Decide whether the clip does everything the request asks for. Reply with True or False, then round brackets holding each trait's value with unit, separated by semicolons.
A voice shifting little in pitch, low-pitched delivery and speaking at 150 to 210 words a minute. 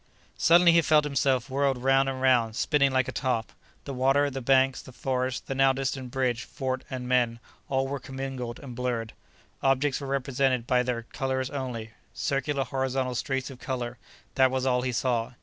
True (1.4 semitones; 130 Hz; 175 wpm)